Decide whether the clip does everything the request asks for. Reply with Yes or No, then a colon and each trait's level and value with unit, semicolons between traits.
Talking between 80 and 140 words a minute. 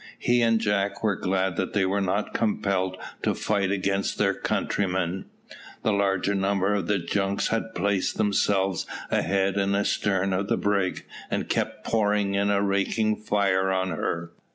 No: average, 160 wpm